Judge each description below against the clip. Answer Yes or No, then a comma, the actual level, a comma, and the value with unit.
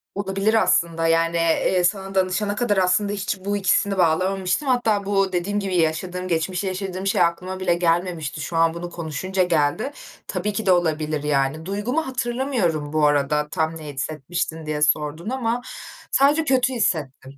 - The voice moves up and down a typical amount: Yes, average, 4.0 semitones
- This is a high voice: No, medium, 180 Hz